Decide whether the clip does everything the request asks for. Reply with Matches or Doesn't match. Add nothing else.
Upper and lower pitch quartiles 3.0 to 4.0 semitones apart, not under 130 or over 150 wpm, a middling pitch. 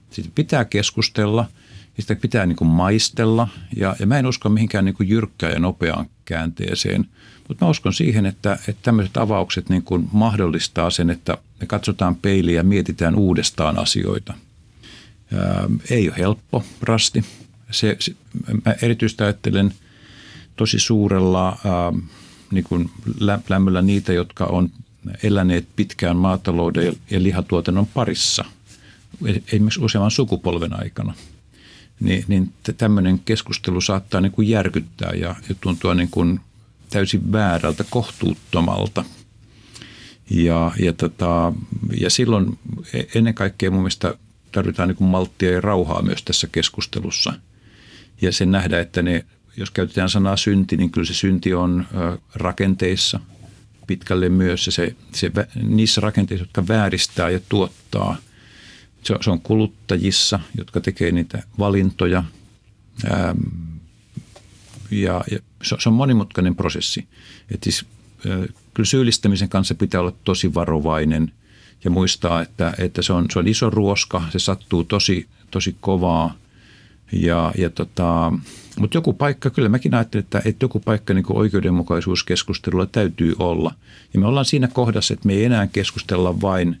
Doesn't match